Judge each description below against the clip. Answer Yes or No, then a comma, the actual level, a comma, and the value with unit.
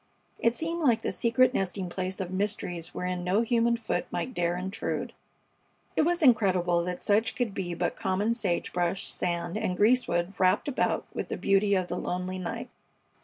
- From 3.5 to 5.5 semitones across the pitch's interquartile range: Yes, average, 4.5 semitones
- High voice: Yes, high, 195 Hz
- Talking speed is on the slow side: No, average, 175 wpm